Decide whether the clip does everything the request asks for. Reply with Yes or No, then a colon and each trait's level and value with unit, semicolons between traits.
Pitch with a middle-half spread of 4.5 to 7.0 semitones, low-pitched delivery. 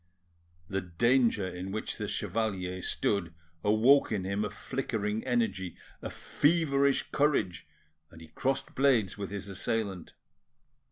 Yes: average, 5.1 semitones; low, 105 Hz